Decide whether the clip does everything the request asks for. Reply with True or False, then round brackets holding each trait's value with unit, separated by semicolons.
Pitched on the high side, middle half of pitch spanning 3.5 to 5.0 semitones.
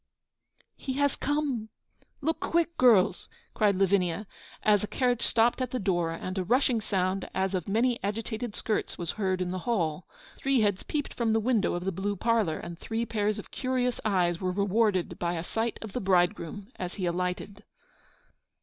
True (205 Hz; 4.2 semitones)